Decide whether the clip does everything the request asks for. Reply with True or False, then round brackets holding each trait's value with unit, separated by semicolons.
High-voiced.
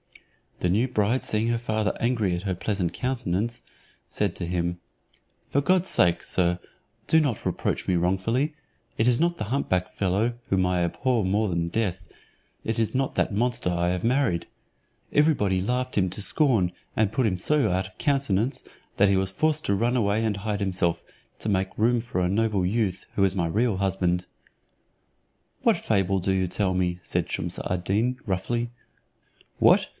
False (100 Hz)